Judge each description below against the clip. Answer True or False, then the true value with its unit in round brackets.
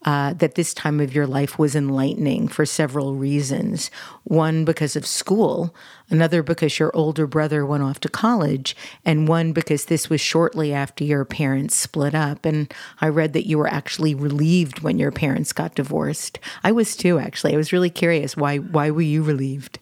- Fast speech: False (190 wpm)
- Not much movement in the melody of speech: True (2.1 semitones)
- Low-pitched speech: False (155 Hz)